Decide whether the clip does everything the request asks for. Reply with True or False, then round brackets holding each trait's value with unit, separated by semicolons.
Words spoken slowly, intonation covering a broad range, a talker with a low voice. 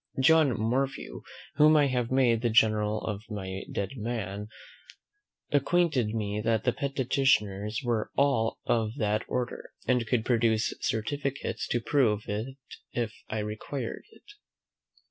False (130 wpm; 3.9 semitones; 115 Hz)